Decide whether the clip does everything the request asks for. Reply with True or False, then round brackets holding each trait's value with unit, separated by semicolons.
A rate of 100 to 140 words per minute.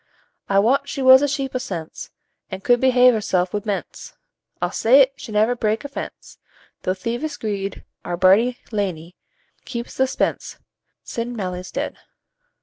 False (155 wpm)